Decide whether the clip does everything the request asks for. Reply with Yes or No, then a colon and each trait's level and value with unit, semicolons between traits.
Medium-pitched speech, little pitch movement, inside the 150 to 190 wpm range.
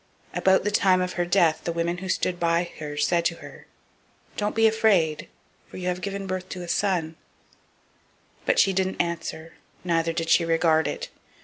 Yes: medium, 175 Hz; narrow, 2.3 semitones; average, 185 wpm